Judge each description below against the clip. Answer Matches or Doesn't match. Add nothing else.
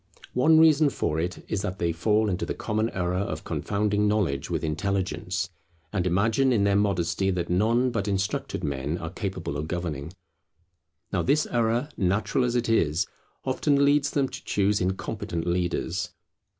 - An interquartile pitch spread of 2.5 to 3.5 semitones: Doesn't match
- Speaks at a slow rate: Doesn't match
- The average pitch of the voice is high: Doesn't match